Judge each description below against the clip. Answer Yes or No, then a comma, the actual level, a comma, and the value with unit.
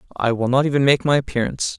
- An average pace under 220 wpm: No, fast, 235 wpm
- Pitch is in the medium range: No, low, 130 Hz